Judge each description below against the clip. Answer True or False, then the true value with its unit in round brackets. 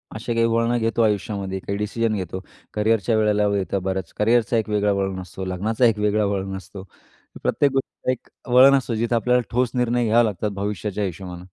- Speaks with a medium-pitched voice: False (105 Hz)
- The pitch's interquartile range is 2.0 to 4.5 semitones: True (2.9 semitones)